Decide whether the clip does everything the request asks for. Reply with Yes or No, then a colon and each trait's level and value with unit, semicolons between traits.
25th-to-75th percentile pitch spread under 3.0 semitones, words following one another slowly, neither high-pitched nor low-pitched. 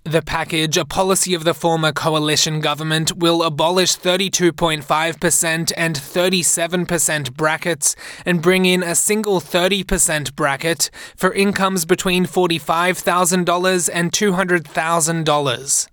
Yes: narrow, 2.4 semitones; slow, 105 wpm; medium, 170 Hz